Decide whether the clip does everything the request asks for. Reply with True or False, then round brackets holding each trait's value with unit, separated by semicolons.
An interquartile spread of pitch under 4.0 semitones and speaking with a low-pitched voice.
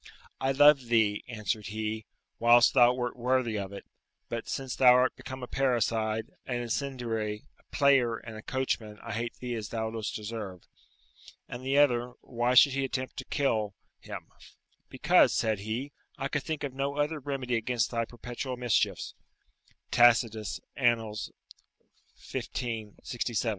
True (2.9 semitones; 120 Hz)